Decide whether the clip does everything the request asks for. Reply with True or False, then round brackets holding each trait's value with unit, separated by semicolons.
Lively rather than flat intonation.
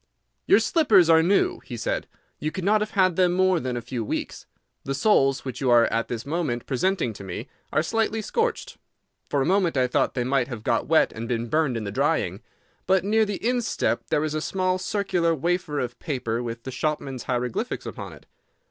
True (7.3 semitones)